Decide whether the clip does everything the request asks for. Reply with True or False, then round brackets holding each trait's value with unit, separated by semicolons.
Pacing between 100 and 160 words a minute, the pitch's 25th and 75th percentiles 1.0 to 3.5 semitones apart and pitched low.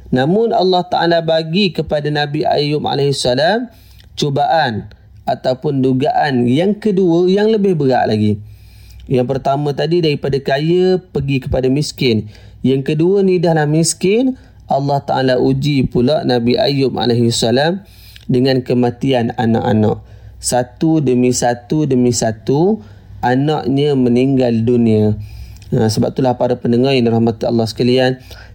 False (120 wpm; 4.4 semitones; 130 Hz)